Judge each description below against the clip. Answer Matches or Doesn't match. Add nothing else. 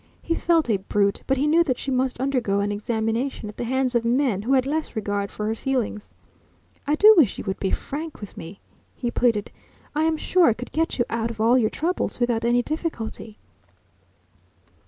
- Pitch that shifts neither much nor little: Matches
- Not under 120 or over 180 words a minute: Doesn't match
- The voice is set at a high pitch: Matches